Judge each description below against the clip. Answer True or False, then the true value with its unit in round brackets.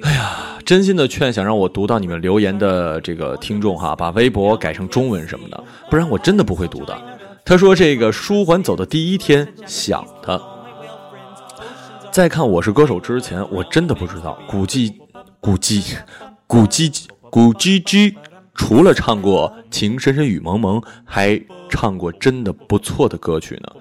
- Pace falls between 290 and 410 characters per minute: False (240 characters per minute)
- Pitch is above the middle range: False (115 Hz)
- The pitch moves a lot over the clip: True (8.2 semitones)